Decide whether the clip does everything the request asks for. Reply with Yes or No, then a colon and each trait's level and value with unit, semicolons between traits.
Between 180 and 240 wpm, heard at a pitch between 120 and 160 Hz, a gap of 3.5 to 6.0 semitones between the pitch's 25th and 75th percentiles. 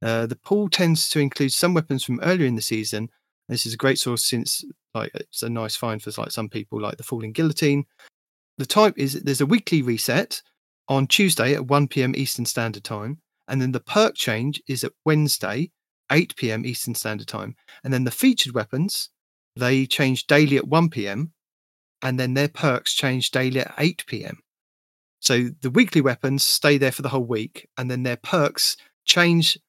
Yes: average, 185 wpm; low, 135 Hz; average, 4.0 semitones